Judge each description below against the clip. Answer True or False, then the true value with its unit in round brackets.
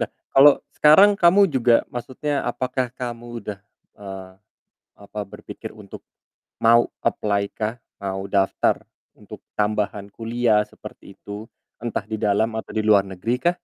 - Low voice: True (110 Hz)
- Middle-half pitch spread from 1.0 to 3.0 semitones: False (3.5 semitones)